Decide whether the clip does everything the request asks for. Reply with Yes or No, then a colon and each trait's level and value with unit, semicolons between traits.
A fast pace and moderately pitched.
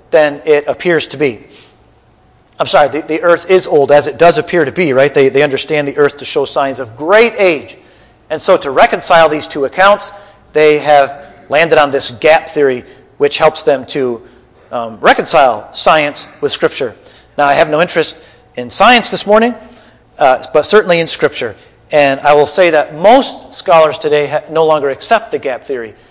No: average, 190 wpm; medium, 155 Hz